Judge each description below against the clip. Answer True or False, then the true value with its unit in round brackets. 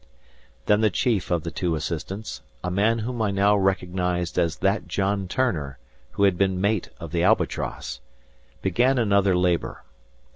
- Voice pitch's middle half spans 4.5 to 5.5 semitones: False (2.8 semitones)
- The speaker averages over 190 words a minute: False (155 wpm)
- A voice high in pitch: False (95 Hz)